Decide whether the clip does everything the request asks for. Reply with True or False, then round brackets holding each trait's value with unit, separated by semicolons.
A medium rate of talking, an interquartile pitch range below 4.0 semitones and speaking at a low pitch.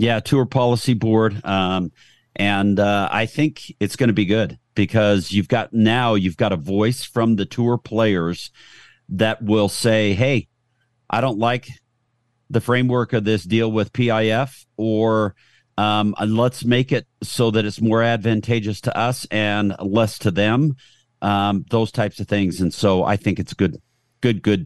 True (170 wpm; 2.9 semitones; 110 Hz)